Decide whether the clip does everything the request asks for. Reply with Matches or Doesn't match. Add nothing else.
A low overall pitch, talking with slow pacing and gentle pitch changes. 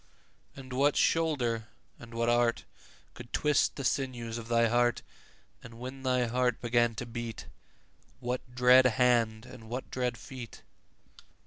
Doesn't match